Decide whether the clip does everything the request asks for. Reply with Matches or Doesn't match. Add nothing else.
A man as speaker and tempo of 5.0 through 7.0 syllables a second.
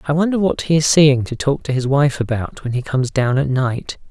Matches